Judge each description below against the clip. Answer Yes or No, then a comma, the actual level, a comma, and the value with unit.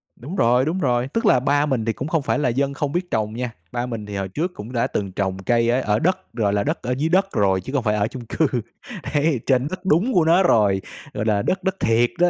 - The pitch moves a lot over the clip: Yes, wide, 6.4 semitones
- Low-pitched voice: Yes, low, 125 Hz